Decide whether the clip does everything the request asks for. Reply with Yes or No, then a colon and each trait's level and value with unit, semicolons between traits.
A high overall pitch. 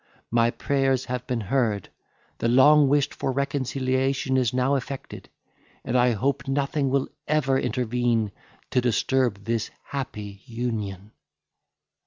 No: low, 125 Hz